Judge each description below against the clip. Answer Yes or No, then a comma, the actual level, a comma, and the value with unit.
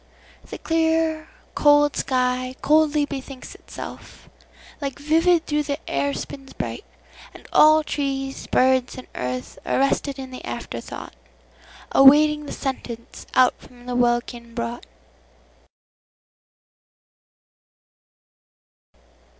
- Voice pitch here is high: Yes, very high, 270 Hz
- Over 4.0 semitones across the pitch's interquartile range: No, average, 3.0 semitones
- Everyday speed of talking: No, slow, 95 wpm